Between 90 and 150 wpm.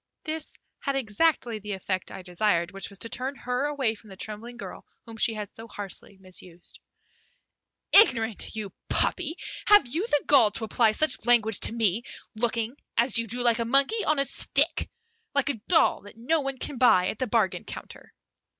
No: average, 185 wpm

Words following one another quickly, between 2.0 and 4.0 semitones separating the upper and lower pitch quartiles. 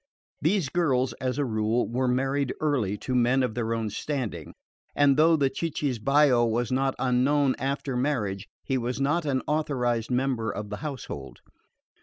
No: average, 160 wpm; average, 3.2 semitones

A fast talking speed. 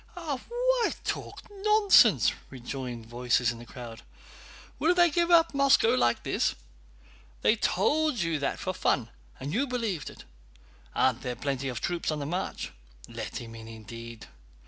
No: average, 150 wpm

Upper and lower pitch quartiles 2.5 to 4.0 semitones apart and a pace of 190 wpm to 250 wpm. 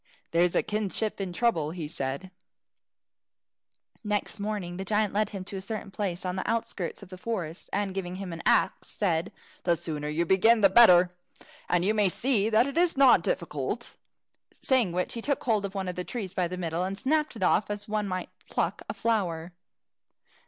Yes: average, 3.4 semitones; average, 195 wpm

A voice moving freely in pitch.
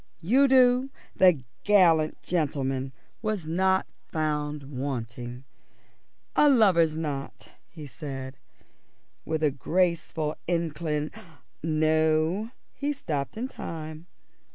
No: average, 4.0 semitones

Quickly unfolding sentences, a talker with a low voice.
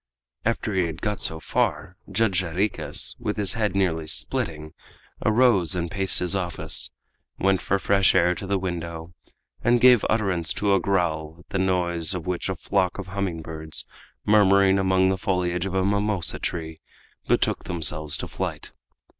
No: average, 165 wpm; very low, 95 Hz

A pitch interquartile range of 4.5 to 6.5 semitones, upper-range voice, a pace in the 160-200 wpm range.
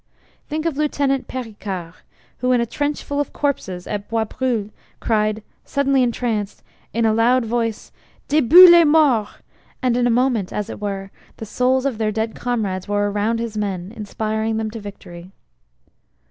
No: average, 3.8 semitones; high, 225 Hz; average, 165 wpm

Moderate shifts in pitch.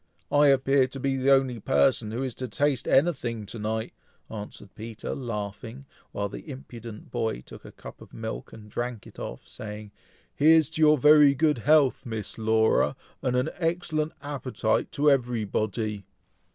Yes: average, 4.2 semitones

